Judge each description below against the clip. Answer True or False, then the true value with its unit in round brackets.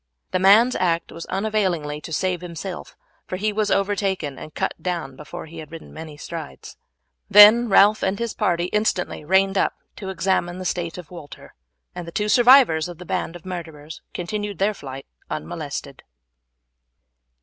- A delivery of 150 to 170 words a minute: True (165 wpm)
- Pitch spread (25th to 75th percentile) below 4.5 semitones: True (3.6 semitones)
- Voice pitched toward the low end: False (180 Hz)